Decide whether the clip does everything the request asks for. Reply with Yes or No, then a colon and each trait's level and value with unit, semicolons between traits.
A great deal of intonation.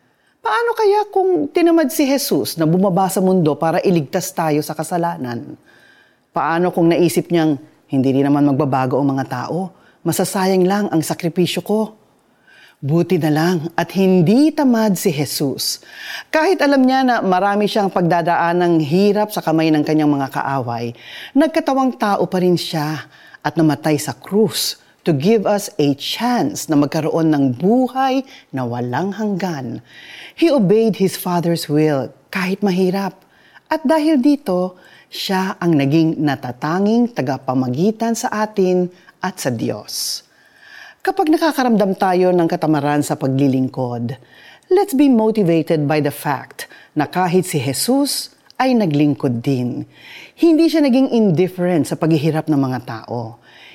Yes: wide, 6.1 semitones